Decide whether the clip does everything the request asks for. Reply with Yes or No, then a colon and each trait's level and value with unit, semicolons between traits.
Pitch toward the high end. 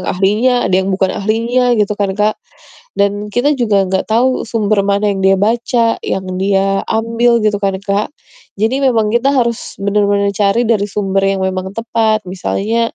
Yes: high, 210 Hz